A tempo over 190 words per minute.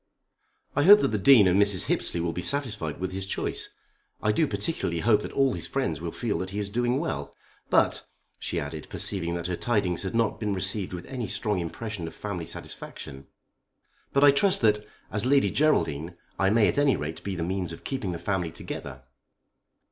Yes: average, 200 wpm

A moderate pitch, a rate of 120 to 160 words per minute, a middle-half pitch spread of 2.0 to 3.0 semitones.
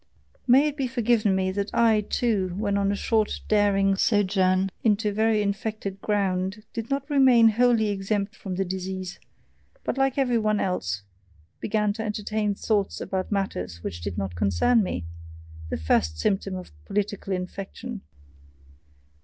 No: high, 205 Hz; average, 150 wpm; average, 2.7 semitones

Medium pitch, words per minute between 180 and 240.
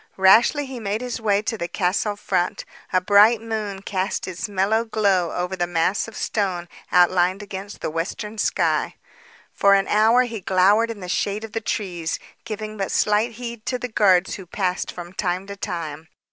No: high, 200 Hz; average, 185 wpm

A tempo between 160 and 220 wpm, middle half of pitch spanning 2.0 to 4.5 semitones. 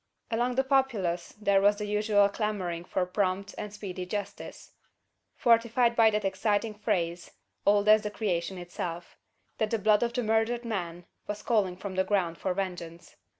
Yes: average, 165 wpm; average, 3.1 semitones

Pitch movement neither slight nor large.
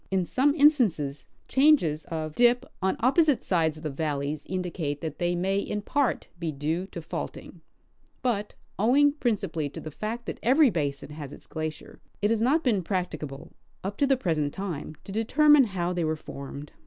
No: wide, 7.5 semitones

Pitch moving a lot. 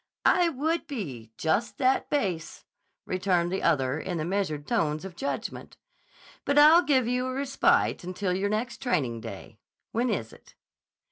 Yes: wide, 8.1 semitones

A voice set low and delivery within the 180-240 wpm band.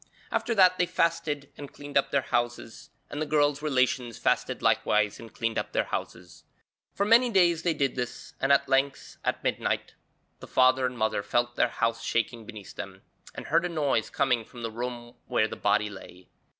Yes: low, 130 Hz; average, 190 wpm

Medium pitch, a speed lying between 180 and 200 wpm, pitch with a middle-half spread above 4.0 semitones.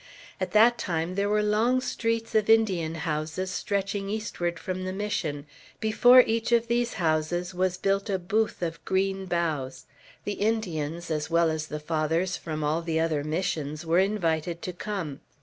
No: medium, 180 Hz; average, 165 wpm; average, 4.5 semitones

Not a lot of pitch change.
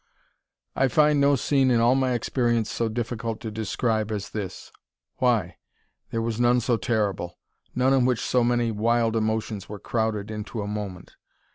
Yes: narrow, 2.3 semitones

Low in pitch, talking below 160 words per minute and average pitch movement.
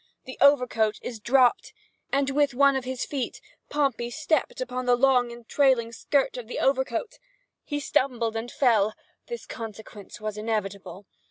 No: very high, 250 Hz; average, 150 wpm; average, 3.4 semitones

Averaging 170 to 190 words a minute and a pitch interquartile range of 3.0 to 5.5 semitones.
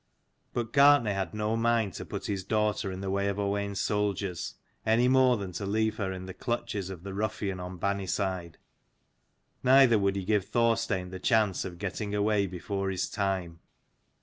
No: average, 180 wpm; narrow, 2.5 semitones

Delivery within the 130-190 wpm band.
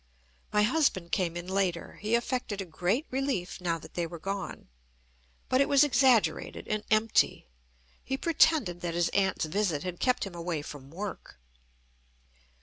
Yes: average, 155 wpm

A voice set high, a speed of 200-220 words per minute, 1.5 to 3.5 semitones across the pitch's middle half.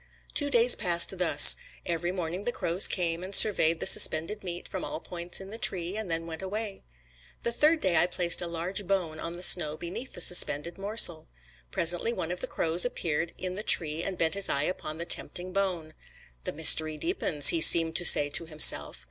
No: medium, 175 Hz; fast, 205 wpm; average, 3.0 semitones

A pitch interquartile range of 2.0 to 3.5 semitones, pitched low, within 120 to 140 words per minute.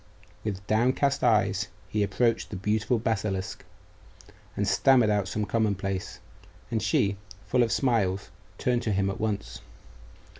Yes: average, 2.9 semitones; low, 105 Hz; slow, 135 wpm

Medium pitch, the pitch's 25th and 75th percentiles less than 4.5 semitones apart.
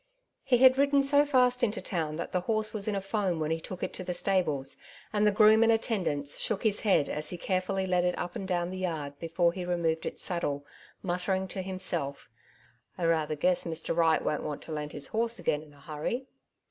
No: medium, 180 Hz; average, 4.8 semitones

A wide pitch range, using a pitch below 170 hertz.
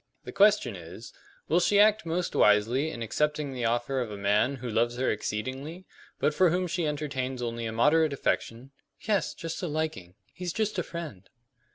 Yes: wide, 6.4 semitones; medium, 140 Hz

